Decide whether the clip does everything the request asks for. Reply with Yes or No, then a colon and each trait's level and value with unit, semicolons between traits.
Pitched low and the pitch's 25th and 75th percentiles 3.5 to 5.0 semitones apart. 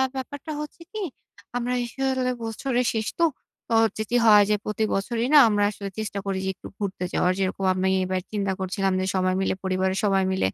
No: high, 205 Hz; average, 4.2 semitones